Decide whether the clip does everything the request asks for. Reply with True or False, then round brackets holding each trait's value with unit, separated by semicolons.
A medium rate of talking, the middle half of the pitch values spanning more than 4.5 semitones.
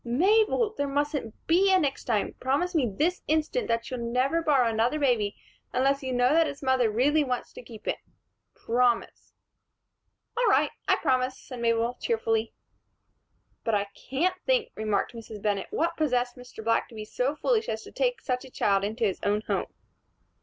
True (180 wpm; 5.0 semitones)